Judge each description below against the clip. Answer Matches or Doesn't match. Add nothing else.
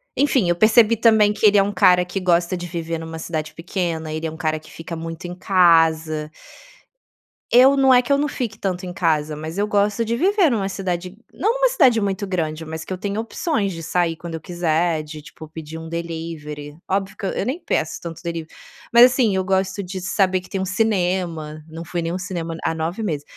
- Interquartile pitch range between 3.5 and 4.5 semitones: Matches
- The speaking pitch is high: Doesn't match